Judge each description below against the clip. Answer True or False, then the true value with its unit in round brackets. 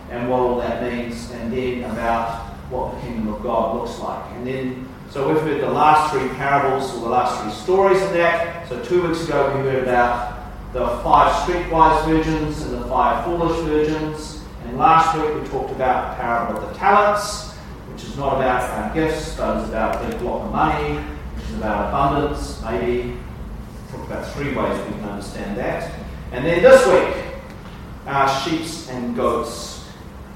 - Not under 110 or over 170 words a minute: False (185 wpm)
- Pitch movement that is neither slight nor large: True (4.8 semitones)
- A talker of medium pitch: False (130 Hz)